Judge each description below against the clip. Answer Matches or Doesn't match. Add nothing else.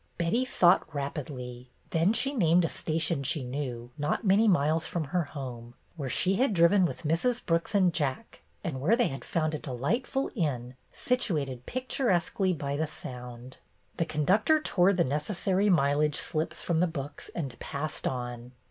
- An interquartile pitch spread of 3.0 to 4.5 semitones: Doesn't match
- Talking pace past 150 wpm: Matches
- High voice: Doesn't match